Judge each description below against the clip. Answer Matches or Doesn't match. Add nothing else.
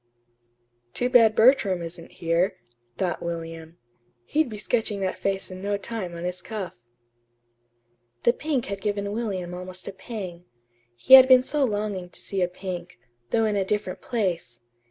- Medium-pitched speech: Doesn't match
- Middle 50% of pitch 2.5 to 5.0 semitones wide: Matches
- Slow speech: Doesn't match